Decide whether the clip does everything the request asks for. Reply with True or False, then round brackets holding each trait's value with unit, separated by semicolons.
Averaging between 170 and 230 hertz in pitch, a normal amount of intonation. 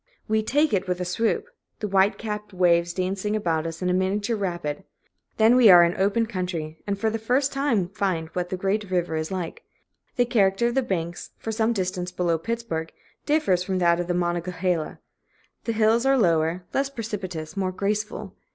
True (190 Hz; 3.8 semitones)